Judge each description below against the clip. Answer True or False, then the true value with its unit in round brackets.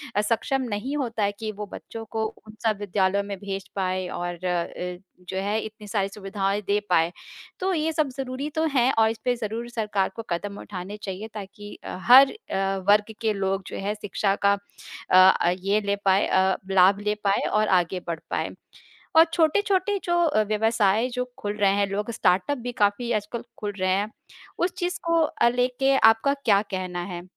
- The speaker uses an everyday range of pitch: True (3.6 semitones)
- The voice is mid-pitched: False (210 Hz)